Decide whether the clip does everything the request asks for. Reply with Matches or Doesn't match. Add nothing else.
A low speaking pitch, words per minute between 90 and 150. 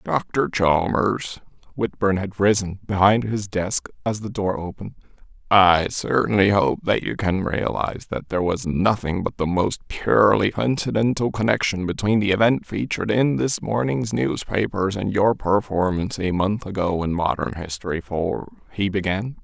Matches